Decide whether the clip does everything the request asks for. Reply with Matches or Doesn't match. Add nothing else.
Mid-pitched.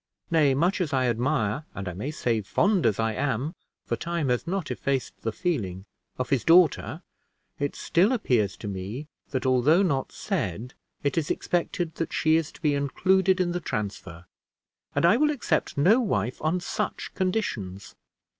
Matches